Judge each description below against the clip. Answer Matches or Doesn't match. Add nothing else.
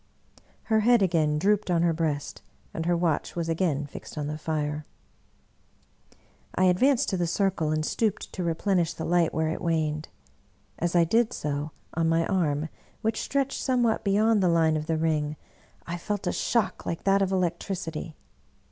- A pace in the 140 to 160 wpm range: Doesn't match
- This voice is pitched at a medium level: Matches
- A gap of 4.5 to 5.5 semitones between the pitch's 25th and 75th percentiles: Doesn't match